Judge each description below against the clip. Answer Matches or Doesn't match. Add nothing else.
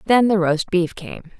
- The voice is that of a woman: Matches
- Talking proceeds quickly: Matches